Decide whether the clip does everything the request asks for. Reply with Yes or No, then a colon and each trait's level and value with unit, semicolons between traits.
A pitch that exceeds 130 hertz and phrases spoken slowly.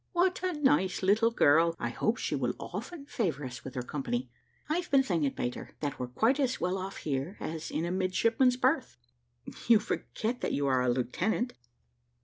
No: high, 190 Hz; average, 185 wpm